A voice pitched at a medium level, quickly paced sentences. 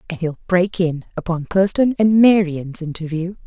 No: medium, 180 Hz; average, 155 wpm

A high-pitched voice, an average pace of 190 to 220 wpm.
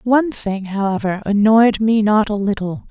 No: high, 210 Hz; average, 165 wpm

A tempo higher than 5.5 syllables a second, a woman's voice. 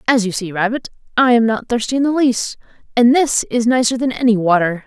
Yes: 5.8 syllables/s; female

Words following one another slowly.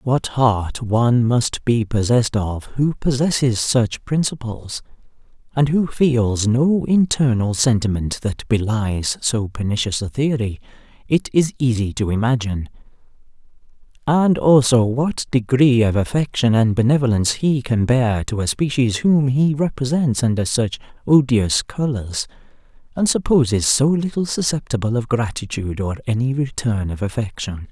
Yes: slow, 130 wpm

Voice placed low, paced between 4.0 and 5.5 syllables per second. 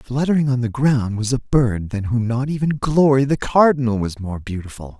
Yes: low, 125 Hz; 5.1 syllables/s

